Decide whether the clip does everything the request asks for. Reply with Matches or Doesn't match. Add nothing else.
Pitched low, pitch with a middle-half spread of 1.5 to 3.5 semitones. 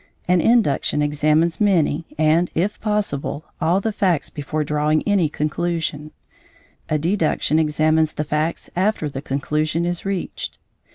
Doesn't match